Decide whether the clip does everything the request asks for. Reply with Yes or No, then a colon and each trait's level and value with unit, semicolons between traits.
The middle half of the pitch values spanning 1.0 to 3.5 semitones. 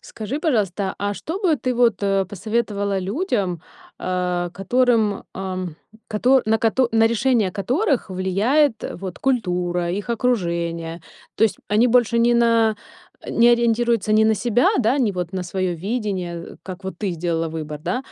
No: average, 4.5 semitones